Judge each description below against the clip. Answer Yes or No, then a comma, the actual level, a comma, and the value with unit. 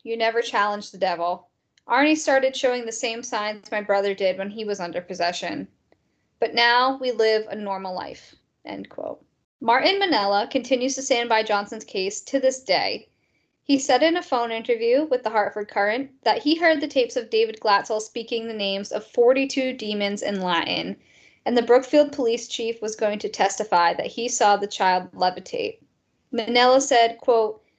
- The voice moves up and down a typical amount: Yes, average, 4.2 semitones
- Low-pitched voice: No, high, 230 Hz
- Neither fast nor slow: Yes, average, 180 wpm